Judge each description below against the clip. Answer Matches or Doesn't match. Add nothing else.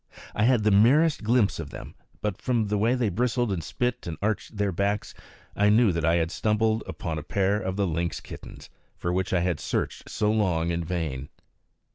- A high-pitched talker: Doesn't match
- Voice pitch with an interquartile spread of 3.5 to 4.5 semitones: Matches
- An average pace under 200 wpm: Doesn't match